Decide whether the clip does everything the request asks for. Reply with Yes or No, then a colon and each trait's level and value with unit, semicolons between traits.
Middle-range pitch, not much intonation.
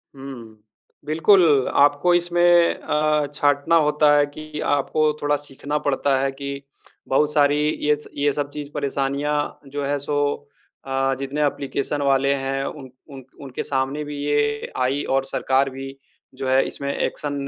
Yes: medium, 145 Hz; narrow, 1.4 semitones